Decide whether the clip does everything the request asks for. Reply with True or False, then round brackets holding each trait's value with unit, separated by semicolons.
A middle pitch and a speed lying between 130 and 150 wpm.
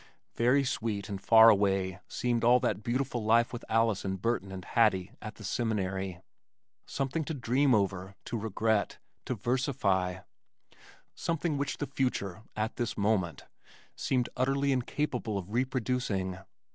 False (115 Hz; 140 wpm)